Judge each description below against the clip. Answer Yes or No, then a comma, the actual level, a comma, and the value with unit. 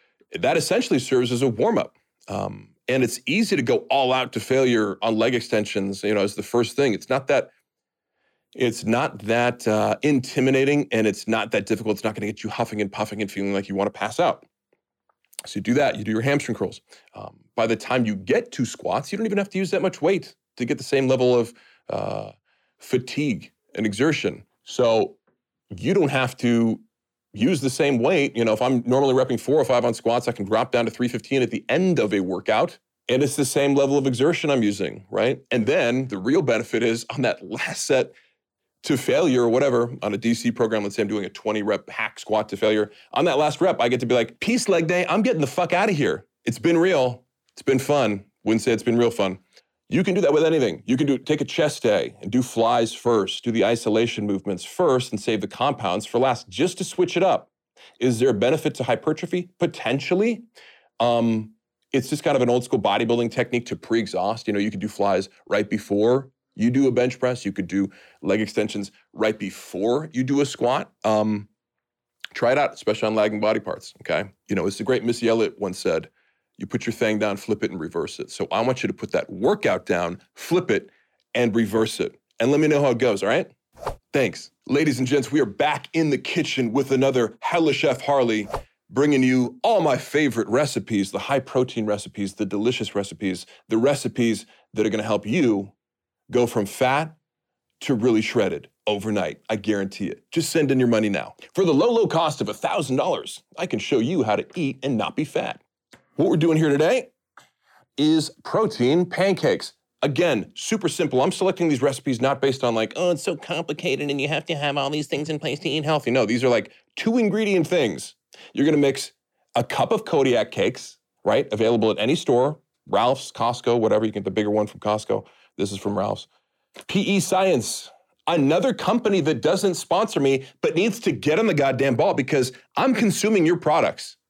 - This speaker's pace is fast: Yes, fast, 215 wpm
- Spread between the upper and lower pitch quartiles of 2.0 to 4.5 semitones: No, average, 5.2 semitones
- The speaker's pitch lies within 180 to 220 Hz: No, low, 125 Hz